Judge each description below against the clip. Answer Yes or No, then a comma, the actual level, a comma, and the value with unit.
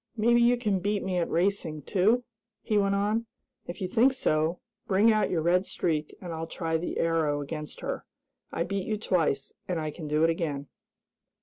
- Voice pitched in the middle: Yes, medium, 180 Hz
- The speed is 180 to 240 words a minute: Yes, average, 195 wpm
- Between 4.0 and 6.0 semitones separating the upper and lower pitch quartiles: Yes, average, 4.3 semitones